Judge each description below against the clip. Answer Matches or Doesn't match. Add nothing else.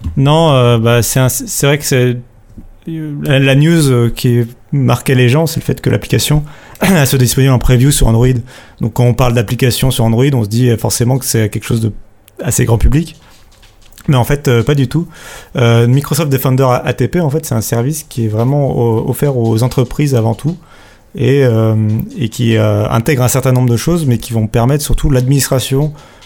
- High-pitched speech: Doesn't match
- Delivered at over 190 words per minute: Matches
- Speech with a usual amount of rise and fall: Matches